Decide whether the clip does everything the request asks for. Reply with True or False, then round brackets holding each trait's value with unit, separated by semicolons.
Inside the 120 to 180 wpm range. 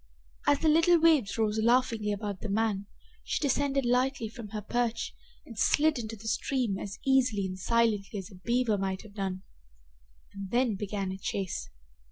True (175 wpm)